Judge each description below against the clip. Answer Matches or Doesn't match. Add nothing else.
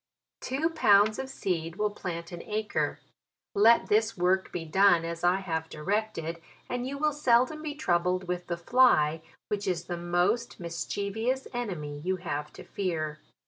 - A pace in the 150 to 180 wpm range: Matches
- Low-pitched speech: Doesn't match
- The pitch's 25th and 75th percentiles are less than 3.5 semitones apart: Doesn't match